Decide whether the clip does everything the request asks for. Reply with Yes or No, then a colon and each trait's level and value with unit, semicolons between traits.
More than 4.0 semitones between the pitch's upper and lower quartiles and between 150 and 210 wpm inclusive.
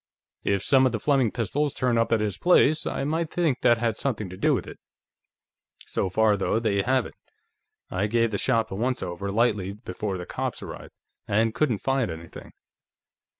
Yes: average, 4.6 semitones; average, 190 wpm